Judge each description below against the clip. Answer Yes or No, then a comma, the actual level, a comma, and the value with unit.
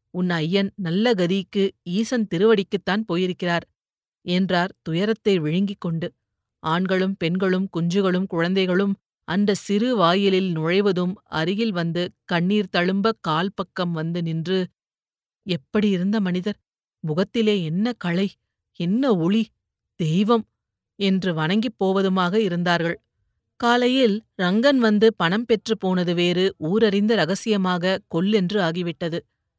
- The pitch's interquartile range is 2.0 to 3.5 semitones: Yes, average, 3.2 semitones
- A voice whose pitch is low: No, medium, 185 Hz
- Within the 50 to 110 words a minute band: Yes, average, 105 wpm